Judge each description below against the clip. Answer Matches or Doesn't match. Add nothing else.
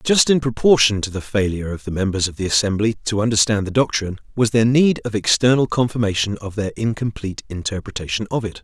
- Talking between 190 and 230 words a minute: Matches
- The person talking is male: Matches